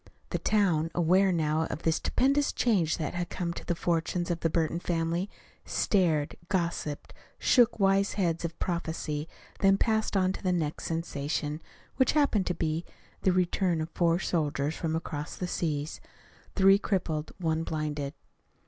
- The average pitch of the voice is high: No, medium, 170 Hz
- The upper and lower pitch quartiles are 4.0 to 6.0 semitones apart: No, average, 3.0 semitones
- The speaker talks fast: No, average, 155 wpm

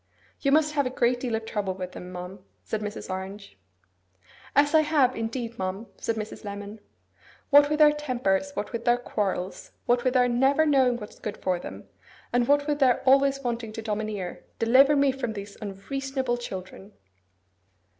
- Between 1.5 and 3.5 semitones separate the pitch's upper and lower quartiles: No, average, 5.0 semitones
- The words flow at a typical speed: Yes, average, 175 wpm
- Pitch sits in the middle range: No, high, 240 Hz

